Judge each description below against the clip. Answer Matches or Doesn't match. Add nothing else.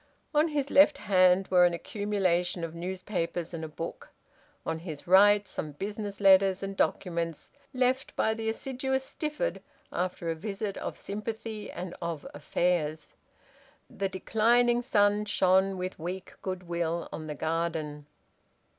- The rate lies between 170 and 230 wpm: Doesn't match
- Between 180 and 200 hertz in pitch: Matches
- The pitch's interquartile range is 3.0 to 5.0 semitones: Matches